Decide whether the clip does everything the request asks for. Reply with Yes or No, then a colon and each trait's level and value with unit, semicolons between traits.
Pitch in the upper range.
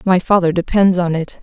No: medium, 180 Hz